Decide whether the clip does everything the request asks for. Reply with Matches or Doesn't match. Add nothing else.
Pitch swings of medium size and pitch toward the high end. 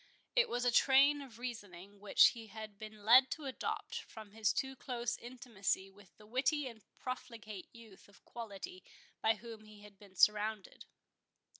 Matches